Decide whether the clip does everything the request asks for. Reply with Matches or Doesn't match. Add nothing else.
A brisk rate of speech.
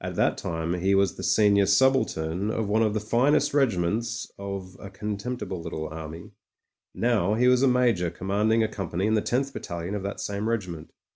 Doesn't match